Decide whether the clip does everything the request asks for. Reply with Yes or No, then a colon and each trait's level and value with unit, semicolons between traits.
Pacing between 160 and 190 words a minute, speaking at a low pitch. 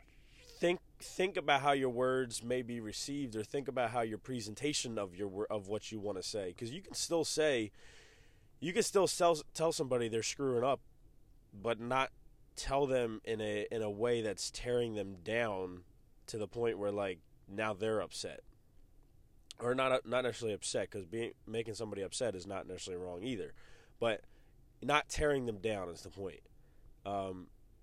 Yes: average, 175 wpm; low, 115 Hz